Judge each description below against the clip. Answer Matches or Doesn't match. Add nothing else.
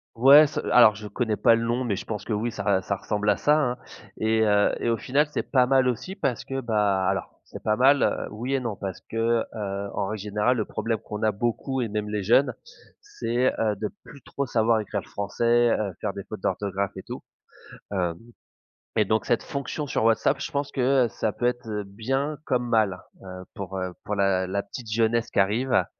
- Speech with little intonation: Doesn't match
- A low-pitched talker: Matches